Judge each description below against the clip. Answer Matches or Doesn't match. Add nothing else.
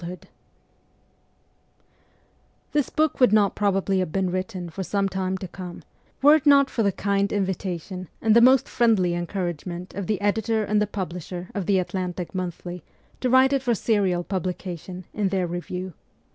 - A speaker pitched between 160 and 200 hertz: Matches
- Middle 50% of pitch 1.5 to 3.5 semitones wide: Matches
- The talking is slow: Doesn't match